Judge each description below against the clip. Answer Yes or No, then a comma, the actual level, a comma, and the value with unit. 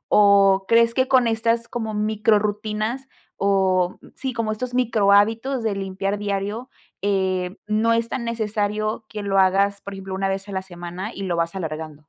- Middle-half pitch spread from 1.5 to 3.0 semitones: Yes, average, 2.7 semitones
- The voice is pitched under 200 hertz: No, high, 205 Hz